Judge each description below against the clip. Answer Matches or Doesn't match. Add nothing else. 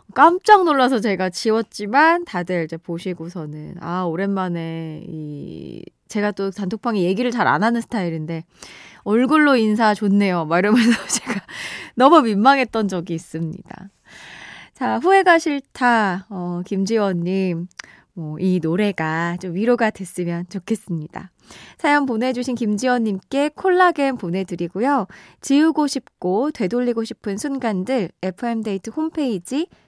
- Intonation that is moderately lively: Doesn't match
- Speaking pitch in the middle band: Doesn't match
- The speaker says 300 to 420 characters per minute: Doesn't match